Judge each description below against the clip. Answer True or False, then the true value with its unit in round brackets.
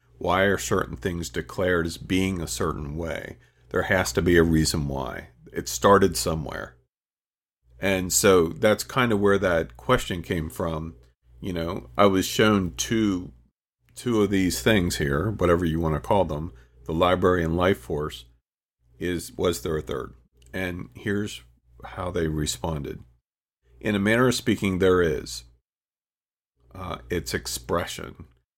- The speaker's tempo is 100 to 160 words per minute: True (150 wpm)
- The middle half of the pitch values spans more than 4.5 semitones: True (4.9 semitones)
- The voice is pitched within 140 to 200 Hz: False (85 Hz)